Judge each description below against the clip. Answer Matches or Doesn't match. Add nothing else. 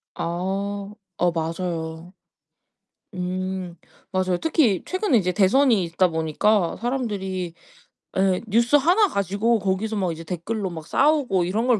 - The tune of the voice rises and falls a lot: Doesn't match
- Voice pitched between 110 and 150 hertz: Doesn't match